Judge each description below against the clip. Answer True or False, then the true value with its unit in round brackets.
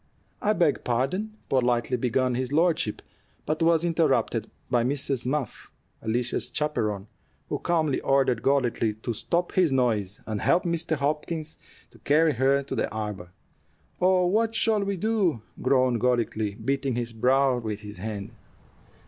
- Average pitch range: False (5.7 semitones)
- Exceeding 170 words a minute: False (150 wpm)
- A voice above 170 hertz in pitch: False (135 Hz)